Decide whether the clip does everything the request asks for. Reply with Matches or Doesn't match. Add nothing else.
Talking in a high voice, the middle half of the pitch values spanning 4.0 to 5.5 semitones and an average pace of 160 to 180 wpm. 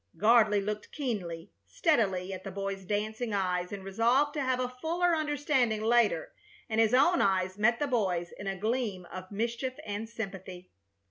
Matches